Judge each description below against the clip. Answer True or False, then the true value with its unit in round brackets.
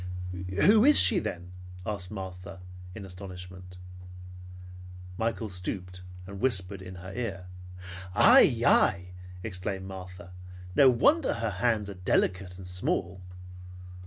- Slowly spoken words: True (115 wpm)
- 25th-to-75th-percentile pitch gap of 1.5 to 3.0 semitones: True (2.7 semitones)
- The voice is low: True (95 Hz)